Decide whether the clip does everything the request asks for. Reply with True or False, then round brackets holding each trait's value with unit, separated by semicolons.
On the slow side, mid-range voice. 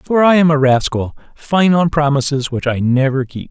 False (205 wpm; 145 Hz)